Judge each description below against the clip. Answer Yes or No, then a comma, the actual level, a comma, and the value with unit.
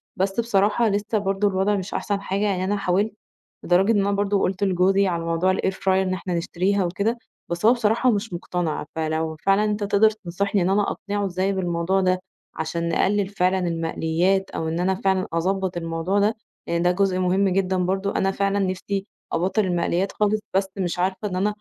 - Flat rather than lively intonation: Yes, narrow, 2.0 semitones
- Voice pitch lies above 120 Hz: Yes, high, 190 Hz